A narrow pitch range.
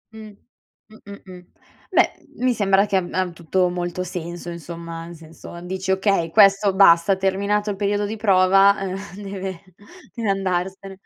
Yes: narrow, 2.2 semitones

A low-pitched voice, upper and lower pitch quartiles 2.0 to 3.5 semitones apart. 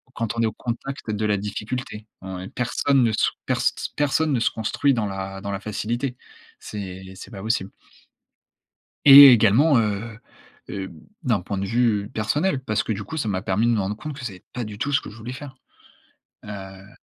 No: low, 110 Hz; average, 3.9 semitones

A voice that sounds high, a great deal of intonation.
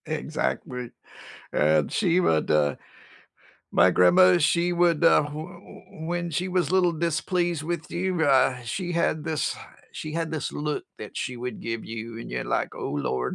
No: medium, 155 Hz; wide, 5.8 semitones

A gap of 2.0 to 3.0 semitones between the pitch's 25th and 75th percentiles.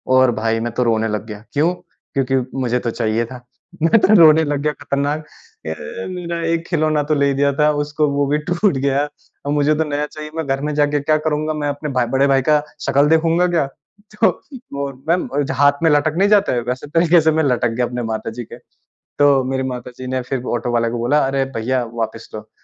No: average, 3.6 semitones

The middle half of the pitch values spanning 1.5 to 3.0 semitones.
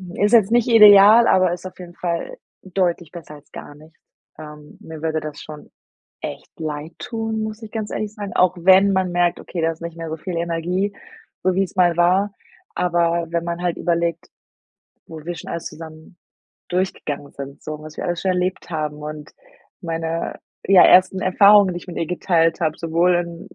Yes: narrow, 2.6 semitones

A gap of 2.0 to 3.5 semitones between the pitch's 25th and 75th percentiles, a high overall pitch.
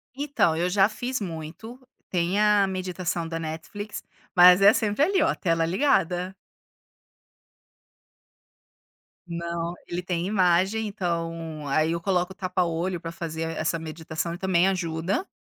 No: average, 2.9 semitones; medium, 180 Hz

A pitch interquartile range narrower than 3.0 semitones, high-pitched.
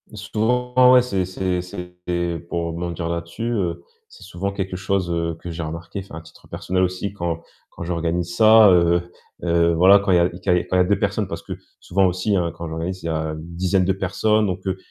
No: narrow, 2.5 semitones; very low, 90 Hz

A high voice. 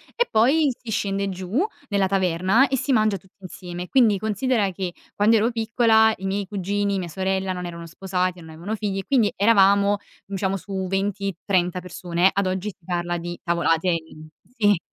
Yes: high, 195 Hz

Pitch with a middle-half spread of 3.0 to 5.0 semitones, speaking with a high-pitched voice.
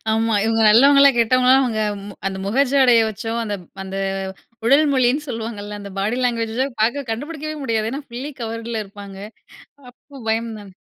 Yes: average, 3.3 semitones; high, 230 Hz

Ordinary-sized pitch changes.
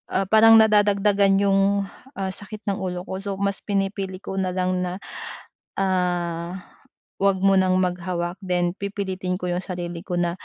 No: narrow, 1.7 semitones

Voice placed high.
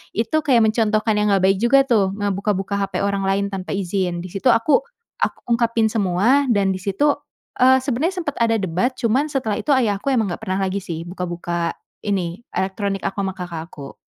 Yes: high, 200 Hz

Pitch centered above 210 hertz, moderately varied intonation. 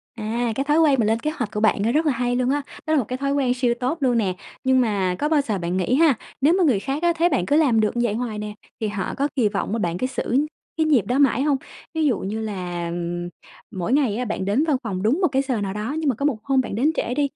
Yes: high, 245 Hz; average, 5.0 semitones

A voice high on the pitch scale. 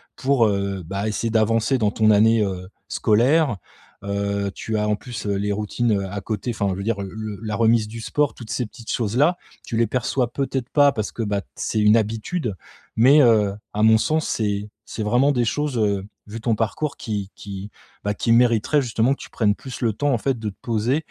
No: low, 110 Hz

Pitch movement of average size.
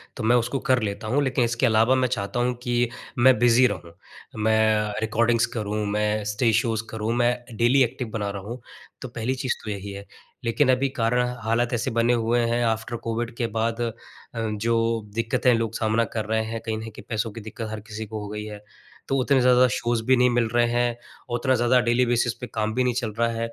No: narrow, 1.7 semitones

